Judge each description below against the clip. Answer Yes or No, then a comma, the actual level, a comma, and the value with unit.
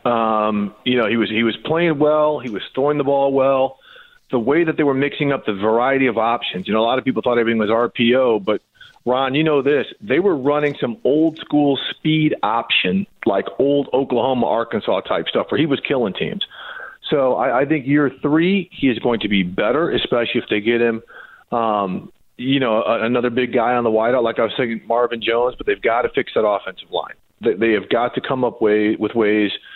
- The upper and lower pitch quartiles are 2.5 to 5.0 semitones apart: Yes, average, 4.2 semitones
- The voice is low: Yes, low, 125 Hz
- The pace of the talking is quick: Yes, fast, 225 wpm